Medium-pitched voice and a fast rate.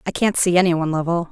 Yes: medium, 170 Hz; fast, 275 wpm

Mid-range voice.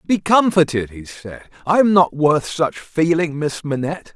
Yes: medium, 155 Hz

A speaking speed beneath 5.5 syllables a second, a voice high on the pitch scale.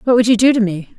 No: 7.1 syllables/s; high, 225 Hz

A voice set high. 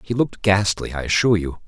No: low, 100 Hz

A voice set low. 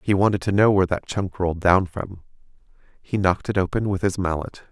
Yes: very low, 95 Hz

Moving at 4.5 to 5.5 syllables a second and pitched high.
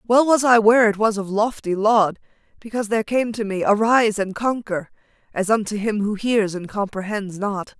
Yes: 5.2 syllables/s; high, 215 Hz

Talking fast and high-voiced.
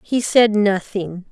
No: slow, 135 wpm; high, 205 Hz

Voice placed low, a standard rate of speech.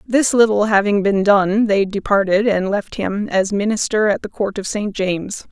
No: high, 205 Hz; average, 195 wpm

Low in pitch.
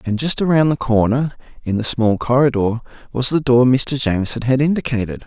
Yes: low, 125 Hz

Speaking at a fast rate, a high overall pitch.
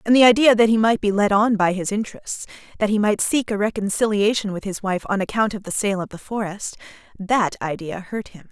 Yes: fast, 225 wpm; high, 205 Hz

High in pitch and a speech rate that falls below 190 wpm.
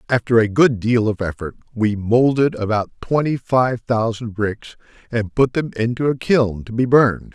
No: low, 115 Hz; average, 180 wpm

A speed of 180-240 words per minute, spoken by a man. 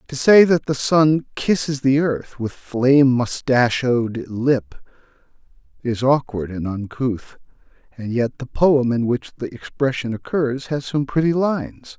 No: average, 145 wpm; male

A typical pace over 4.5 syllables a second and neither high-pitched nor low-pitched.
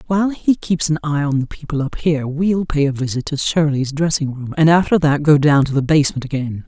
Yes: 5.8 syllables/s; medium, 150 Hz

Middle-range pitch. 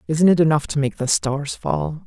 Yes: medium, 150 Hz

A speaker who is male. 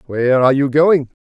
Yes: male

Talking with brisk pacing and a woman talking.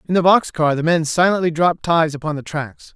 No: fast, 245 wpm; male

